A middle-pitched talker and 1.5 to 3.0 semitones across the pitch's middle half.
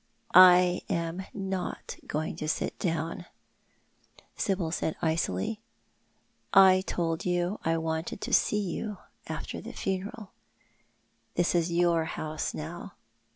Yes: medium, 175 Hz; narrow, 2.5 semitones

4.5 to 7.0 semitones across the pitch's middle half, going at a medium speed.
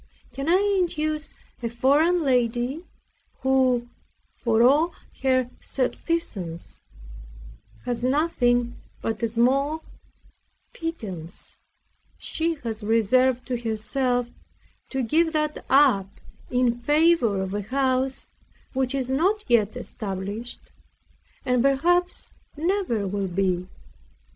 No: average, 4.8 semitones; slow, 100 wpm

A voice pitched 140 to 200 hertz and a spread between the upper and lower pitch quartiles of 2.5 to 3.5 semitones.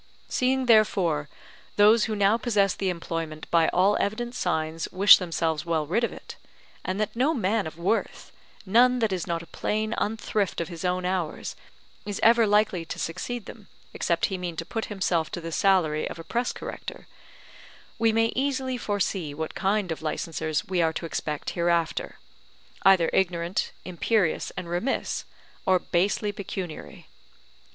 No: high, 190 Hz; average, 4.5 semitones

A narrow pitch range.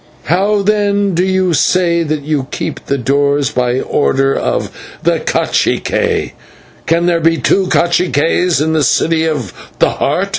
No: average, 4.2 semitones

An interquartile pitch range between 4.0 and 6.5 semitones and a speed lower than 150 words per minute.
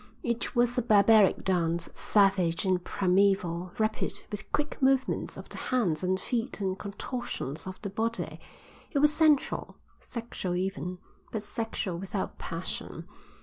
Yes: average, 4.3 semitones; average, 140 wpm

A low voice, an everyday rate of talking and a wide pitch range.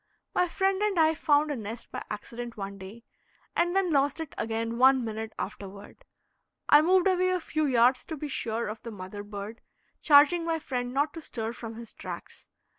No: very high, 255 Hz; average, 190 wpm; wide, 6.3 semitones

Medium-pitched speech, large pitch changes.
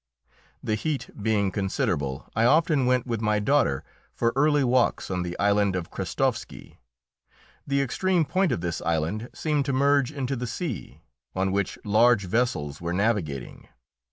No: low, 115 Hz; wide, 6.5 semitones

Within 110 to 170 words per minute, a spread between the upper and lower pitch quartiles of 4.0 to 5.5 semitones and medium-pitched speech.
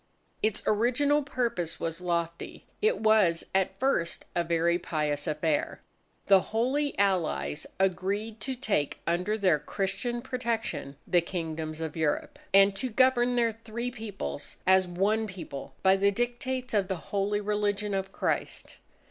No: average, 140 wpm; average, 5.1 semitones; high, 195 Hz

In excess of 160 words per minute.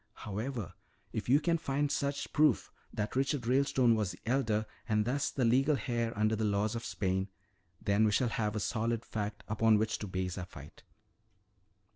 Yes: average, 180 wpm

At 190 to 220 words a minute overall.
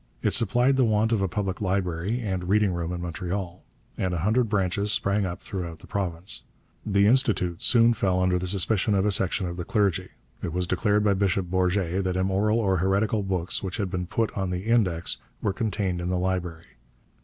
Yes: average, 200 wpm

